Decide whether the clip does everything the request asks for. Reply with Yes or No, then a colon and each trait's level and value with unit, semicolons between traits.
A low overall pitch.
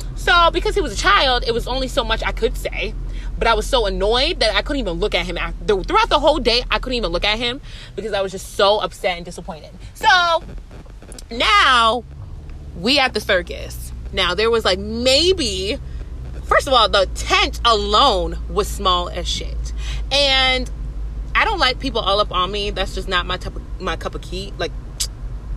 No: high, 215 Hz